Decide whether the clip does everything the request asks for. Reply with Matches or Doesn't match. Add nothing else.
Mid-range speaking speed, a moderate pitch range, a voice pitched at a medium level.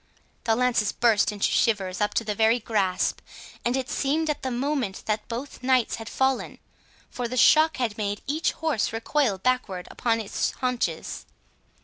Doesn't match